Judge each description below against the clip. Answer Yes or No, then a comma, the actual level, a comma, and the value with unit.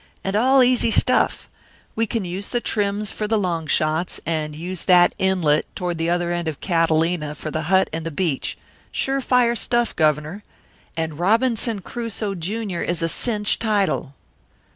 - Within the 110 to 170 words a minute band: Yes, average, 165 wpm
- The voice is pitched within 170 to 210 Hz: Yes, medium, 185 Hz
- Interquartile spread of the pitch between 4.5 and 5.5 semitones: Yes, average, 5.0 semitones